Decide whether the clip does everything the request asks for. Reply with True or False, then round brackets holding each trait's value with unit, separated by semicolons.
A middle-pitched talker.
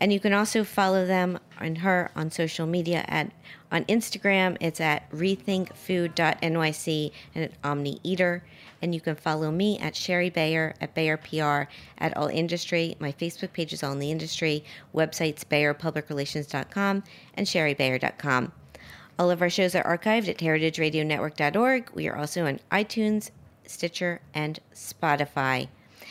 True (165 Hz)